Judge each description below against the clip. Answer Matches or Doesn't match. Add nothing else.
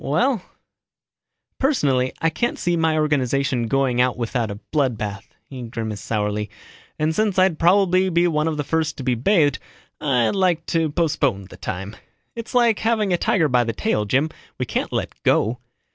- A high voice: Doesn't match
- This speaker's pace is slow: Doesn't match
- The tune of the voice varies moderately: Doesn't match